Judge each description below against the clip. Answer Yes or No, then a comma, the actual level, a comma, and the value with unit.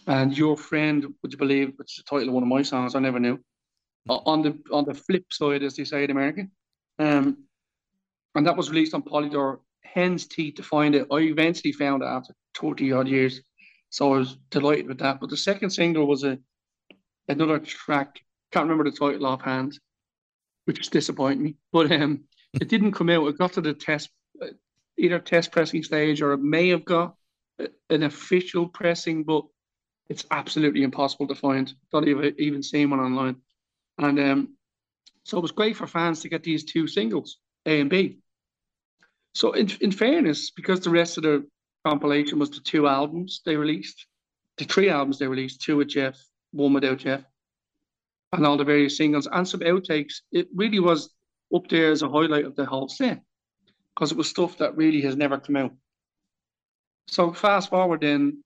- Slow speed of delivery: No, average, 190 wpm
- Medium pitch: Yes, medium, 150 Hz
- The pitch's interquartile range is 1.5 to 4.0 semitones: Yes, average, 3.3 semitones